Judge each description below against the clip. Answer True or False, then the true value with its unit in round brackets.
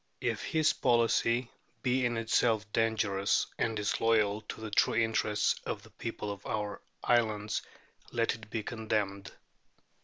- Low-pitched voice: True (110 Hz)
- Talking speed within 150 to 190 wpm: False (135 wpm)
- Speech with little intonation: True (1.9 semitones)